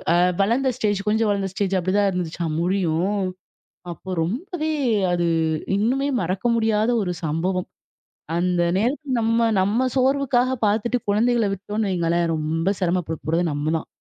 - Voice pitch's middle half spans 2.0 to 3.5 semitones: No, average, 4.8 semitones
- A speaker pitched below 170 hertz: No, high, 200 Hz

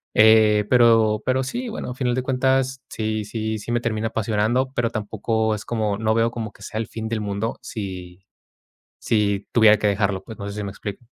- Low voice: Yes, low, 110 Hz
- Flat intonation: Yes, narrow, 2.2 semitones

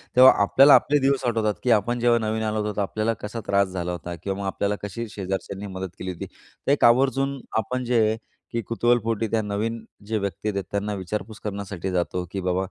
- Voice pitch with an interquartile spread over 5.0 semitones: No, average, 3.1 semitones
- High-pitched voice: No, low, 105 Hz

